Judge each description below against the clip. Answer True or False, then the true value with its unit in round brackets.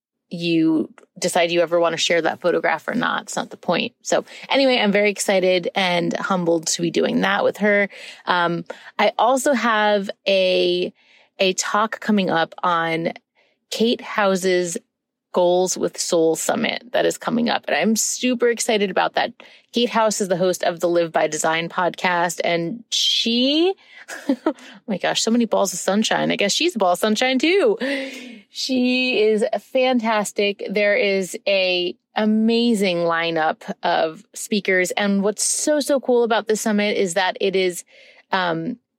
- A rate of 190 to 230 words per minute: False (165 wpm)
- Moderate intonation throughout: True (4.9 semitones)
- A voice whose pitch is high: True (205 Hz)